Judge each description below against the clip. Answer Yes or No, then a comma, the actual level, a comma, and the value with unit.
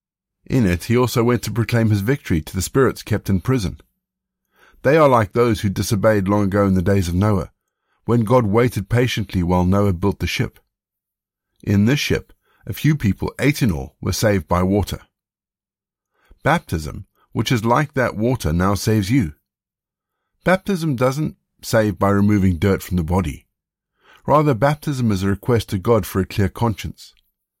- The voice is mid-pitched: No, low, 105 Hz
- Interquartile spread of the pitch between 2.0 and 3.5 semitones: No, average, 4.3 semitones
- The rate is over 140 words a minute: Yes, average, 170 wpm